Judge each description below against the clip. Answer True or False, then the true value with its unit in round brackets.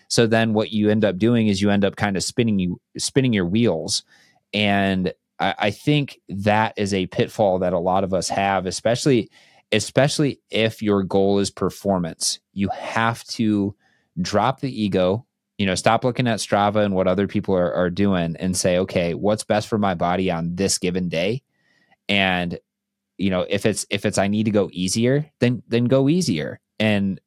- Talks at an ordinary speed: True (190 wpm)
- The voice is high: False (105 Hz)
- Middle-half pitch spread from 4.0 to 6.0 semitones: False (2.9 semitones)